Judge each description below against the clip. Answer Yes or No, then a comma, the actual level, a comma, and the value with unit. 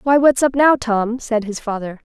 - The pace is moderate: No, fast, 225 wpm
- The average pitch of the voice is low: No, high, 240 Hz